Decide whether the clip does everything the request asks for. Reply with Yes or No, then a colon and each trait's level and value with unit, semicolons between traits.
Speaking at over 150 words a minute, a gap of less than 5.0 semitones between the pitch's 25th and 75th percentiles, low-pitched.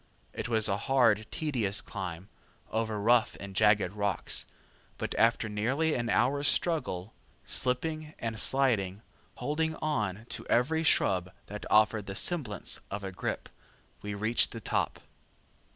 No: slow, 135 wpm; average, 4.6 semitones; low, 110 Hz